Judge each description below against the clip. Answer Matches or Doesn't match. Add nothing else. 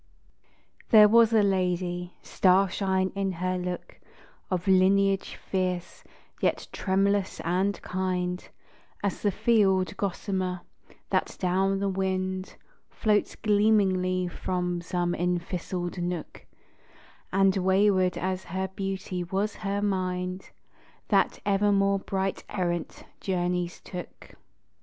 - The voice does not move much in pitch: Matches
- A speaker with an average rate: Doesn't match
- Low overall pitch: Doesn't match